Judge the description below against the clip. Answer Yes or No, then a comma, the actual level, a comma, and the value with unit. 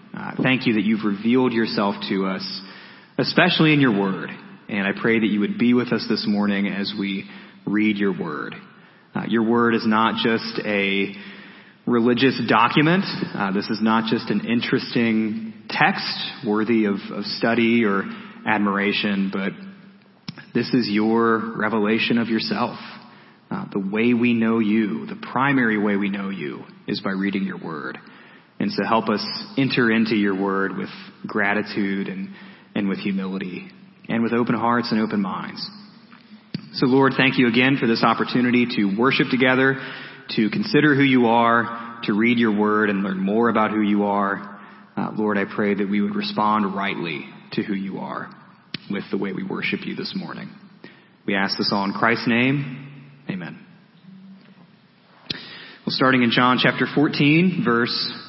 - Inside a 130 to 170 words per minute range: Yes, average, 165 wpm